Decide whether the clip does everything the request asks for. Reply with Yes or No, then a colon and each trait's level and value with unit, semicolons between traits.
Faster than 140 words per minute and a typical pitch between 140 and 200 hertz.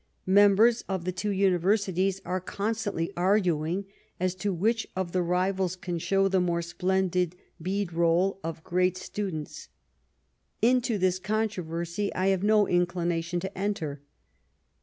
No: slow, 135 wpm; medium, 185 Hz